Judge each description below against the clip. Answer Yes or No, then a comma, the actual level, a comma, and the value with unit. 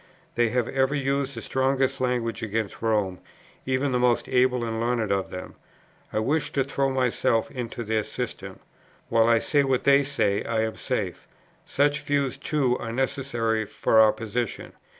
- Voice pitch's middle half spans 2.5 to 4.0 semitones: Yes, average, 3.2 semitones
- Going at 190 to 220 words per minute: No, average, 170 wpm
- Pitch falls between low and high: No, low, 125 Hz